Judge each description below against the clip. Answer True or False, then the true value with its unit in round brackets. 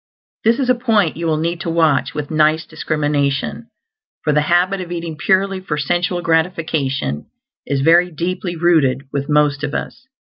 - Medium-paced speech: True (170 wpm)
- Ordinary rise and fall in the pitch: True (3.0 semitones)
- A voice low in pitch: False (165 Hz)